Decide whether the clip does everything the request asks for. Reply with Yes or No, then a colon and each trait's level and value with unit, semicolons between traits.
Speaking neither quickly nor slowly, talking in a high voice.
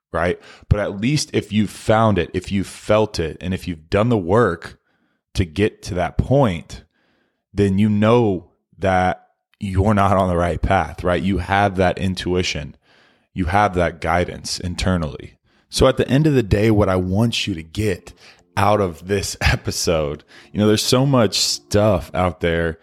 No: average, 180 wpm; very low, 95 Hz